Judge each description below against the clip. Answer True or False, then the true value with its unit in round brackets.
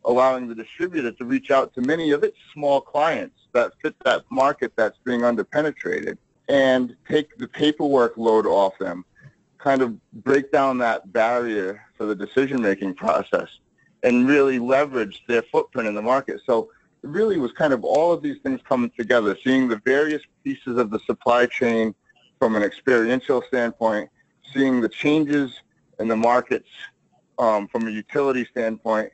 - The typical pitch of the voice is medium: False (130 Hz)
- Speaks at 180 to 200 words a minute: False (165 wpm)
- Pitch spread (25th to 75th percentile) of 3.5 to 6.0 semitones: True (4.5 semitones)